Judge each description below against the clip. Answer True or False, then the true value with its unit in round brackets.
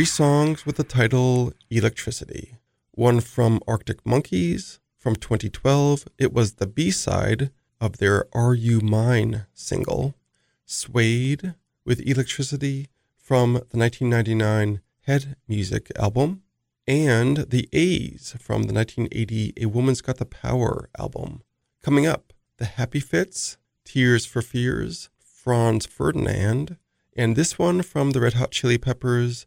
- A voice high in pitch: False (120 Hz)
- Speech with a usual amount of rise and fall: True (3.4 semitones)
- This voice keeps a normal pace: False (130 wpm)